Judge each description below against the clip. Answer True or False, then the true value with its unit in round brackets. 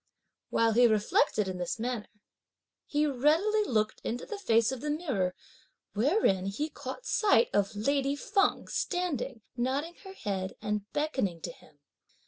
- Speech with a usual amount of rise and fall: False (6.4 semitones)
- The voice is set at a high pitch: True (250 Hz)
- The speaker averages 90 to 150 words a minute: True (145 wpm)